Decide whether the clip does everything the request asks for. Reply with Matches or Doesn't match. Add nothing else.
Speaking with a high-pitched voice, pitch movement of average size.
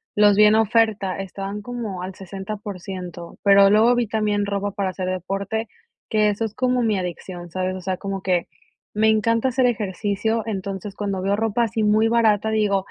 Doesn't match